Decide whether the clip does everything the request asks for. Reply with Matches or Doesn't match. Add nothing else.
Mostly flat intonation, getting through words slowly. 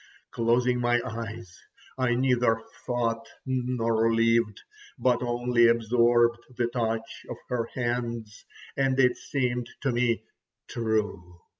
Matches